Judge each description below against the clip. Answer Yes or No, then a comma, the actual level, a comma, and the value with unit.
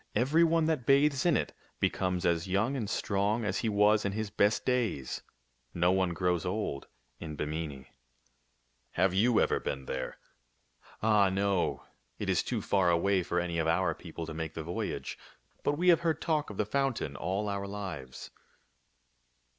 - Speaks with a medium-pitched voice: No, low, 100 Hz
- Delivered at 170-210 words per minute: Yes, average, 185 wpm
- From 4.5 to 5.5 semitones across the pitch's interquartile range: Yes, average, 4.9 semitones